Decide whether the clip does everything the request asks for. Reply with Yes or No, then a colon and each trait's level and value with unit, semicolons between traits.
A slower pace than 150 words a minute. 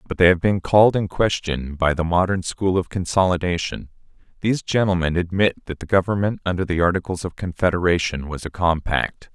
No: average, 175 wpm